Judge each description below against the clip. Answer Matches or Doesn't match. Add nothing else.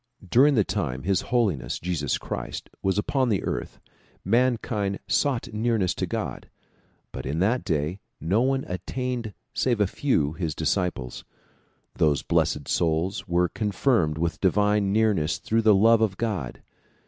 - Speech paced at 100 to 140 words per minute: Doesn't match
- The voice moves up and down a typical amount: Doesn't match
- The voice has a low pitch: Matches